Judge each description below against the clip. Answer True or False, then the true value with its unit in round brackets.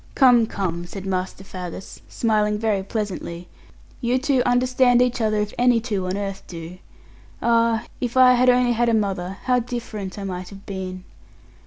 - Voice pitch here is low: False (215 Hz)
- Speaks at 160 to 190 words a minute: True (170 wpm)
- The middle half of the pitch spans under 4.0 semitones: False (4.3 semitones)